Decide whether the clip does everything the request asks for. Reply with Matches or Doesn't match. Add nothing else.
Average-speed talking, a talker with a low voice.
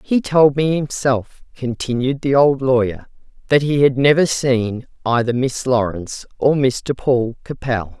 Matches